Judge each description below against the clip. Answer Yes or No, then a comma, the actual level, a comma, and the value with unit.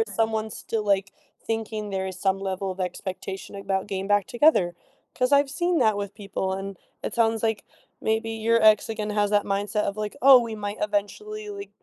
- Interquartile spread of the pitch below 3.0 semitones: Yes, narrow, 2.4 semitones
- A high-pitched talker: Yes, high, 210 Hz